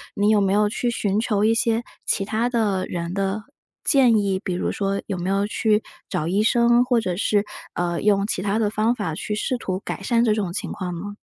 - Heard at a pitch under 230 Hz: Yes, high, 205 Hz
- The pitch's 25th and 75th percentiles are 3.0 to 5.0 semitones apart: No, narrow, 2.5 semitones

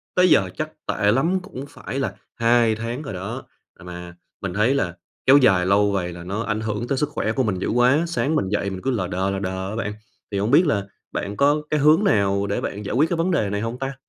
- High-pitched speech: No, low, 110 Hz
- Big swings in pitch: Yes, wide, 5.8 semitones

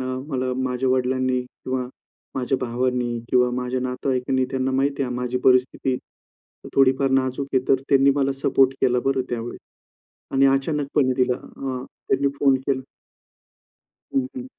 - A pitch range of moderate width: No, narrow, 1.2 semitones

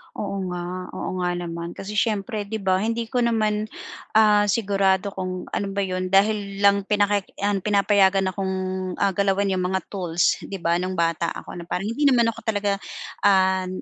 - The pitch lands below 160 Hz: No, high, 195 Hz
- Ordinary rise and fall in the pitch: No, narrow, 2.0 semitones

